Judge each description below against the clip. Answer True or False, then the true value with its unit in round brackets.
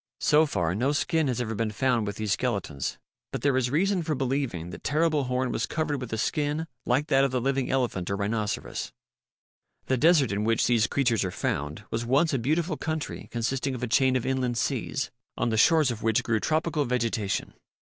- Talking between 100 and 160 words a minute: False (205 wpm)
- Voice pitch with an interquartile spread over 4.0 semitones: True (4.4 semitones)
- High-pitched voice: False (125 Hz)